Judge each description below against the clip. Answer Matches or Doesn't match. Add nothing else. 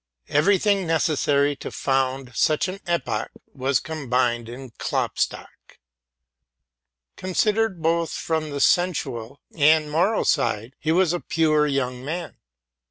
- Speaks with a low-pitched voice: Doesn't match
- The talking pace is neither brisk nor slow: Doesn't match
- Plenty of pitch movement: Doesn't match